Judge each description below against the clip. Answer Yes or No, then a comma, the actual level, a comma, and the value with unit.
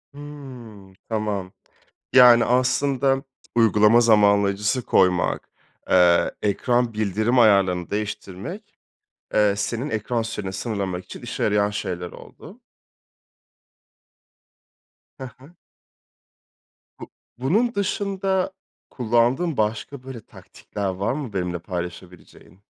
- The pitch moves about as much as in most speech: Yes, average, 4.6 semitones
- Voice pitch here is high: No, low, 110 Hz